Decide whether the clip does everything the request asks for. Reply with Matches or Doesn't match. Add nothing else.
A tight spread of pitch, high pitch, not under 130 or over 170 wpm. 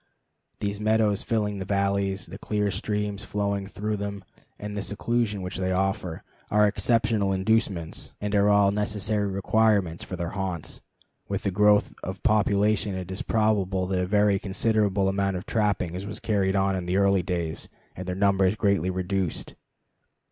Doesn't match